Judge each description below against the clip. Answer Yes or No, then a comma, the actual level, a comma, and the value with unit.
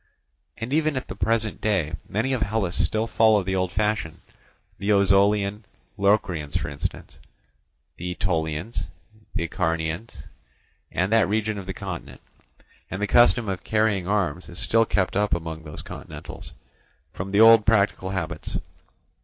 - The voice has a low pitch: Yes, low, 100 Hz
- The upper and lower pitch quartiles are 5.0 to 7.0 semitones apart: No, average, 3.6 semitones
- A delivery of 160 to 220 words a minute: No, average, 145 wpm